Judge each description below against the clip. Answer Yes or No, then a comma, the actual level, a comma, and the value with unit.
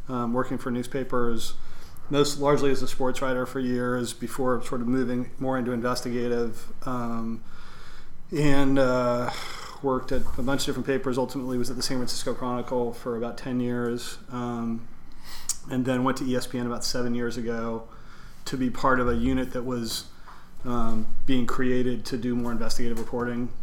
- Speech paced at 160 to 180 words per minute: Yes, average, 170 wpm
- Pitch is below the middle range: Yes, low, 125 Hz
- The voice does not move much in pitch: Yes, narrow, 1.5 semitones